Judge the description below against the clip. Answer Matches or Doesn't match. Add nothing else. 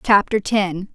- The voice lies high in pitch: Matches